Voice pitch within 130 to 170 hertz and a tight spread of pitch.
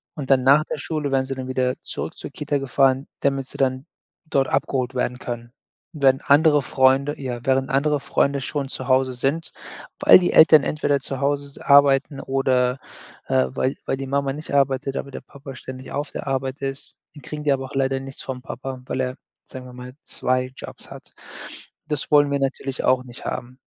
Yes: low, 135 Hz; narrow, 1.4 semitones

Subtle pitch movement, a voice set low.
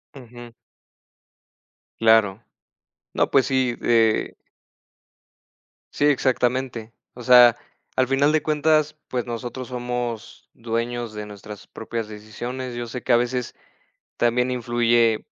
Yes: narrow, 1.9 semitones; low, 120 Hz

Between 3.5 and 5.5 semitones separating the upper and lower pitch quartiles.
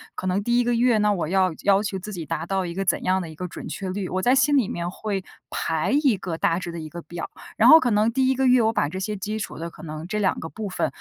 Yes: average, 4.0 semitones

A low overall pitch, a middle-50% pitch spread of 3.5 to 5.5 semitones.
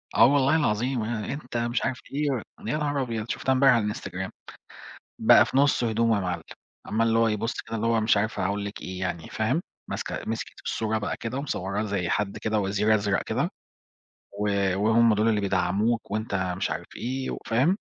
No: low, 110 Hz; average, 3.0 semitones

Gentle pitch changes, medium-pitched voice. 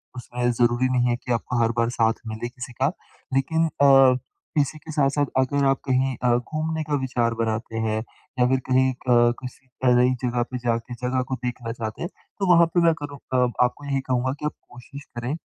No: narrow, 2.3 semitones; low, 125 Hz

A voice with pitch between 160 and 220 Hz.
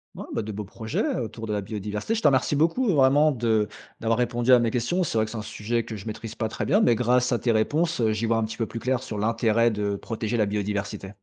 No: low, 115 Hz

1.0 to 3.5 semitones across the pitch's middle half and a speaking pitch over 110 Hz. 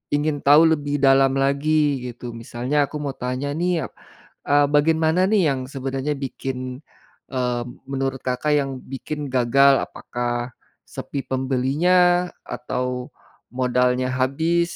Yes: narrow, 2.5 semitones; low, 135 Hz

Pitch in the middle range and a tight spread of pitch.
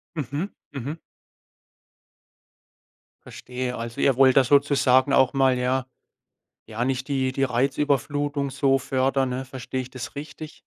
No: low, 130 Hz; narrow, 1.6 semitones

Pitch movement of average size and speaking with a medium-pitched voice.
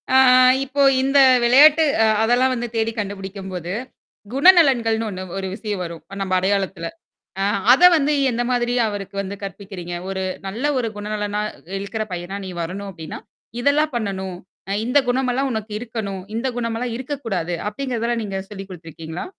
No: average, 4.3 semitones; high, 210 Hz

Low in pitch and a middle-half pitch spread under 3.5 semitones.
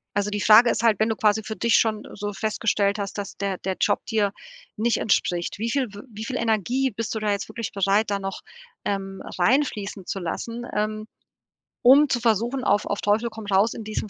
No: high, 215 Hz; narrow, 2.4 semitones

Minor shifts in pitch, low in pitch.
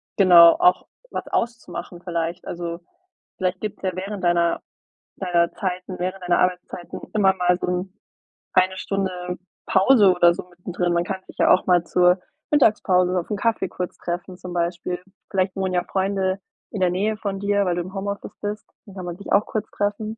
No: narrow, 1.9 semitones; medium, 185 Hz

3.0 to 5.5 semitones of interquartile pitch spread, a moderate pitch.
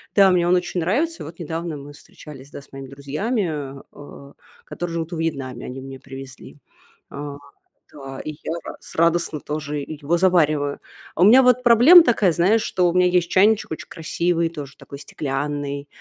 Yes: average, 4.1 semitones; medium, 160 Hz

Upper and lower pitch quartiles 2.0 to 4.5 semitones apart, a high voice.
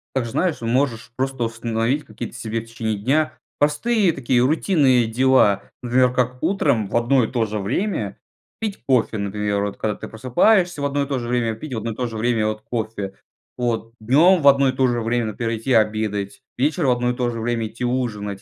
No: average, 3.2 semitones; low, 120 Hz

